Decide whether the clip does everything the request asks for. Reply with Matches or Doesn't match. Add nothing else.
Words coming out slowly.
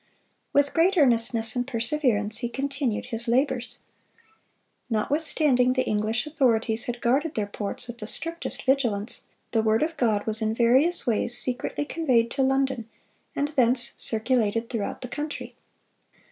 Doesn't match